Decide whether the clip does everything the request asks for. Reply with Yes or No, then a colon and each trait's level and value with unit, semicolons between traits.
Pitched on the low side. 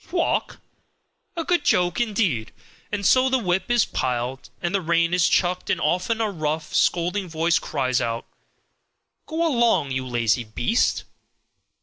No: medium, 175 Hz